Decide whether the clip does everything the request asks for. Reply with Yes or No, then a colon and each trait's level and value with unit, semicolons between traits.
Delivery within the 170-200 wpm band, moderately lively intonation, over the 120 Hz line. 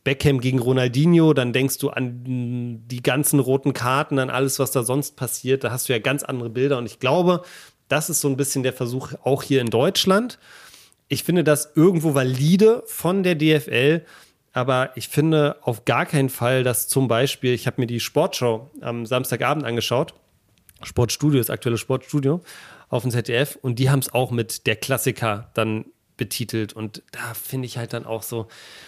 Yes: average, 185 wpm; average, 3.0 semitones; low, 130 Hz